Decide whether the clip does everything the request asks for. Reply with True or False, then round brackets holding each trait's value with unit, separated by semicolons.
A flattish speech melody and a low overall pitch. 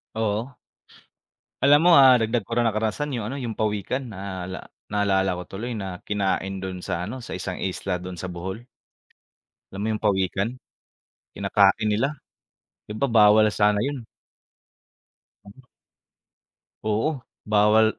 False (3.2 semitones; 105 Hz)